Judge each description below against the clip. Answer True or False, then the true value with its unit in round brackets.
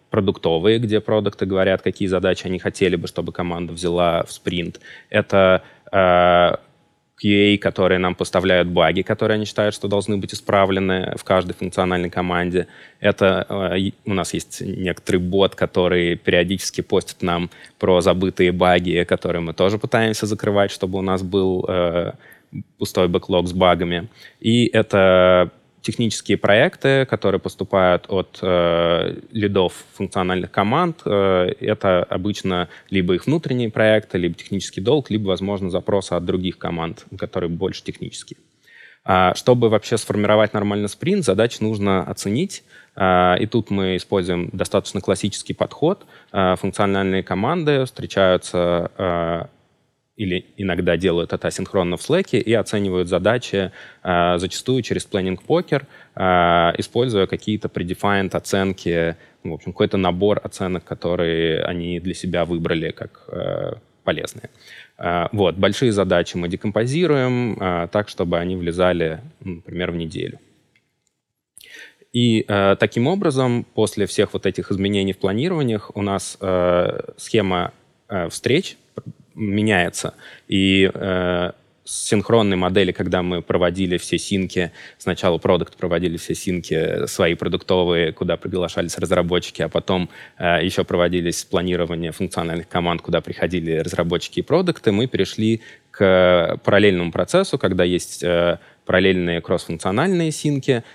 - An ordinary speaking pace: True (130 wpm)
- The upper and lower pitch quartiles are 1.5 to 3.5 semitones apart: True (2.9 semitones)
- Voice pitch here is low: True (95 Hz)